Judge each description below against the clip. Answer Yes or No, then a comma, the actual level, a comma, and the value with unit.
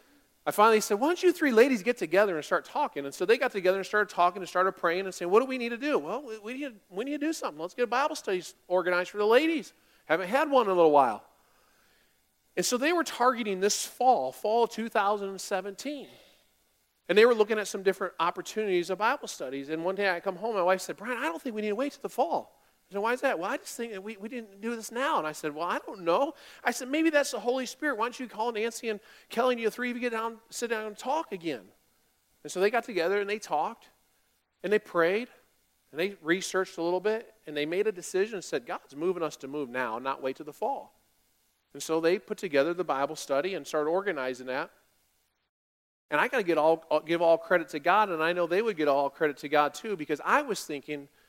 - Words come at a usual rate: No, fast, 255 wpm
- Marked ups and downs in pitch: Yes, wide, 6.6 semitones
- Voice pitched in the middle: No, high, 200 Hz